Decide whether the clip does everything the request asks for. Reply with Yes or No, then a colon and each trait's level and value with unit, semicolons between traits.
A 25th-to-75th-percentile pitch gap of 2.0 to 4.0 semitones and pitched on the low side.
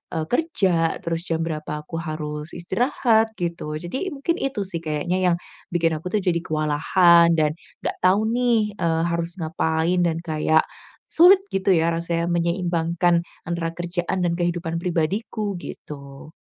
No: narrow, 2.5 semitones; medium, 170 Hz